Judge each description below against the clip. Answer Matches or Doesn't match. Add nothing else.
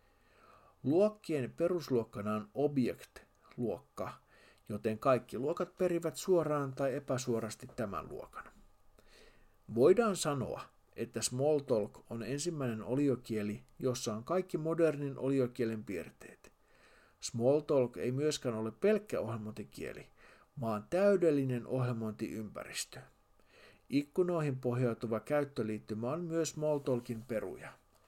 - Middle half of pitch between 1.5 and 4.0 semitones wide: Doesn't match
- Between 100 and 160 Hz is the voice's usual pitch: Matches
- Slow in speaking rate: Matches